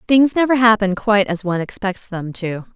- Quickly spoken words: No, average, 195 wpm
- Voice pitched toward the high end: Yes, high, 210 Hz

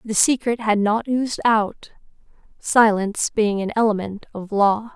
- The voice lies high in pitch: Yes, high, 215 Hz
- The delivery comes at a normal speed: Yes, average, 145 wpm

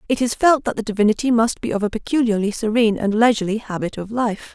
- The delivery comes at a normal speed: No, fast, 225 wpm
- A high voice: Yes, high, 220 Hz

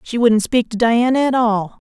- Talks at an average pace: No, fast, 220 wpm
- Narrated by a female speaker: Yes, female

